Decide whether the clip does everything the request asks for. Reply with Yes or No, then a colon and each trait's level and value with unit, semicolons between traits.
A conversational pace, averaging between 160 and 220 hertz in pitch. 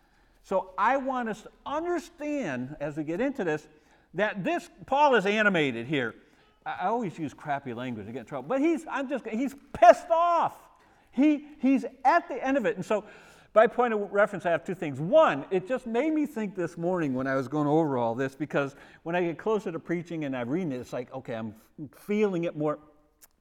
No: fast, 215 wpm; medium, 185 Hz